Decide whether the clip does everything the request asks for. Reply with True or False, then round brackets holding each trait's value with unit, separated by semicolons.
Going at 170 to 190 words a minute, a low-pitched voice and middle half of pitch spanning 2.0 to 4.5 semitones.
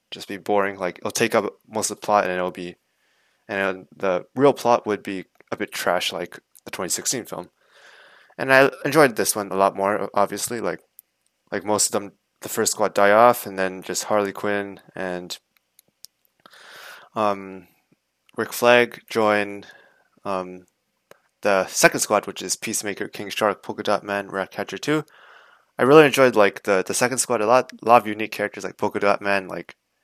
True (180 wpm; 100 Hz; 3.6 semitones)